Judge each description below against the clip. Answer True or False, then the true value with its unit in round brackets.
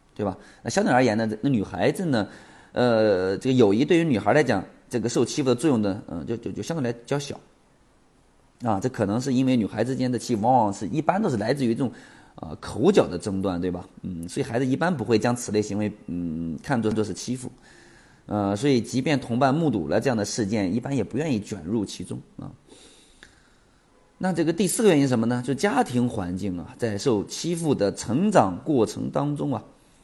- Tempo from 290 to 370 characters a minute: True (310 characters per minute)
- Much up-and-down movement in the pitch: False (4.6 semitones)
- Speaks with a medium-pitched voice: False (120 Hz)